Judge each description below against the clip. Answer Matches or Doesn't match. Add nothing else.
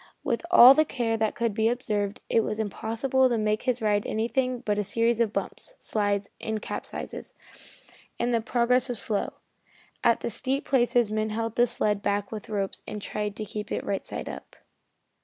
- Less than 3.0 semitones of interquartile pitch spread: Matches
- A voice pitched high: Matches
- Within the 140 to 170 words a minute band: Doesn't match